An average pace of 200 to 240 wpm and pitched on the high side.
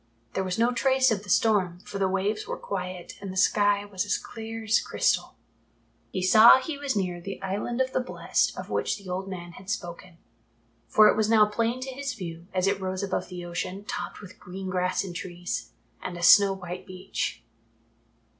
Yes: fast, 205 wpm; high, 195 Hz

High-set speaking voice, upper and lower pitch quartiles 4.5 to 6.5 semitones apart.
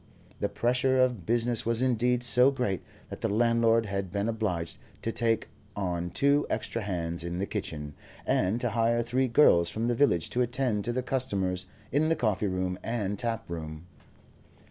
No: low, 115 Hz; average, 4.9 semitones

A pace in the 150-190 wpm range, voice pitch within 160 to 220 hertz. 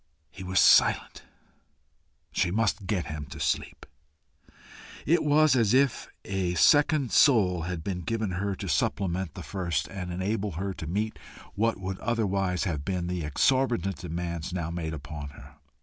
No: average, 155 wpm; very low, 95 Hz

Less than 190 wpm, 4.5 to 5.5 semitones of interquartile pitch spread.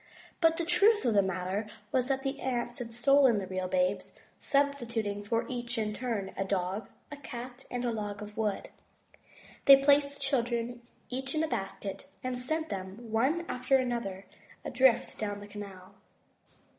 Yes: average, 170 wpm; average, 4.8 semitones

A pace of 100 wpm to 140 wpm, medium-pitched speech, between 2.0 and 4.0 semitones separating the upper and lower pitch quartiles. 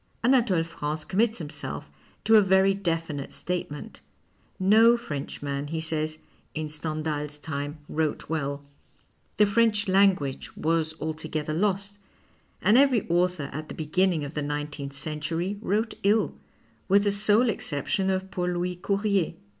No: slow, 135 wpm; medium, 170 Hz; average, 4.8 semitones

